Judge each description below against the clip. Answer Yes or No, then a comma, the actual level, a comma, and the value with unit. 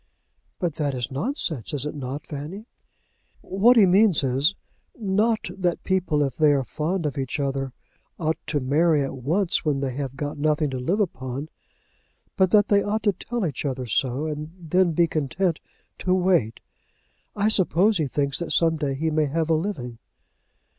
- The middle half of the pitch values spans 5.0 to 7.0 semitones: Yes, average, 5.3 semitones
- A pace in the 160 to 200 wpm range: Yes, average, 180 wpm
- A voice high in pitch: No, medium, 155 Hz